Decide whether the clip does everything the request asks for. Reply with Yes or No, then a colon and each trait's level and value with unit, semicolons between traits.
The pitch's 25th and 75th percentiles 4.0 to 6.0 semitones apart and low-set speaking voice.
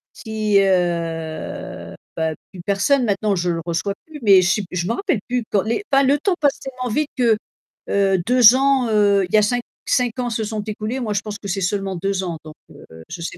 No: average, 4.7 semitones; high, 210 Hz